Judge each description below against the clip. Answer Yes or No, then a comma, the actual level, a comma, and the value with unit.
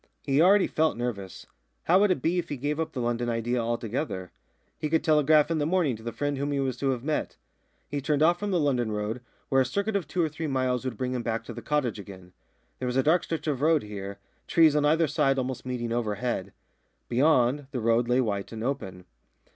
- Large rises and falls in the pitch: No, average, 4.6 semitones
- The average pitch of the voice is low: Yes, low, 130 Hz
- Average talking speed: No, fast, 235 wpm